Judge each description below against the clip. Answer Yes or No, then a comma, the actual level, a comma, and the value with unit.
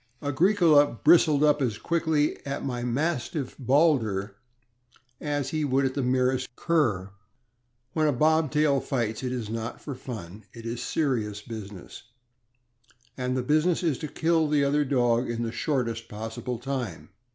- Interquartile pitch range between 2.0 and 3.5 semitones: No, average, 4.3 semitones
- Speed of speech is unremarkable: Yes, average, 155 wpm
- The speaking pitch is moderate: No, low, 130 Hz